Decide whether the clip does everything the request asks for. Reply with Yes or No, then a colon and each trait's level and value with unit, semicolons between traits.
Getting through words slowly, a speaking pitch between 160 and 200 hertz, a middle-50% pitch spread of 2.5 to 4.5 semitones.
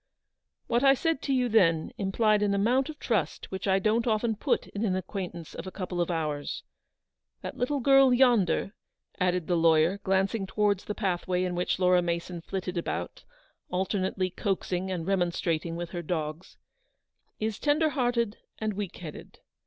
No: average, 170 wpm; high, 190 Hz; average, 4.0 semitones